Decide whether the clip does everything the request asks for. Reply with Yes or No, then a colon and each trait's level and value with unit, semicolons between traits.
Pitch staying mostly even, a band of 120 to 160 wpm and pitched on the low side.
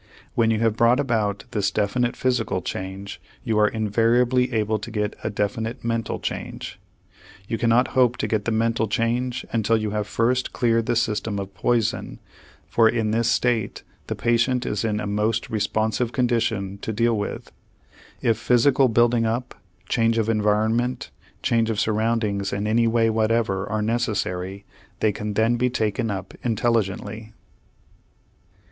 Yes: narrow, 1.9 semitones; average, 155 wpm; low, 115 Hz